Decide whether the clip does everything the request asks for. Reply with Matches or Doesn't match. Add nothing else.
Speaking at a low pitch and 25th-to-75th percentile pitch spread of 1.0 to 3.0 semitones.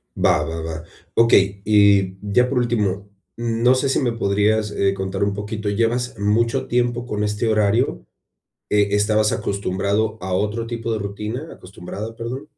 Matches